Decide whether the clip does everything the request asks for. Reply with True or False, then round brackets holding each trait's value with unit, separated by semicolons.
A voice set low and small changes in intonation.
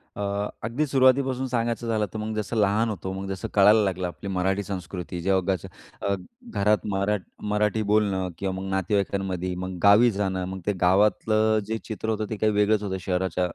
True (100 Hz; 2.3 semitones)